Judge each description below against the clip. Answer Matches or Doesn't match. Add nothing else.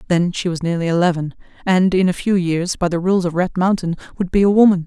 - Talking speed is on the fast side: Matches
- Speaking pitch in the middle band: Matches